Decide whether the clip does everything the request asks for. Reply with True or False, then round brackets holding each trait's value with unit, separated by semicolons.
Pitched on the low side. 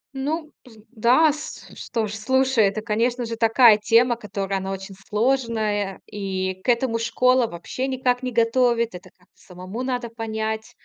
False (230 Hz)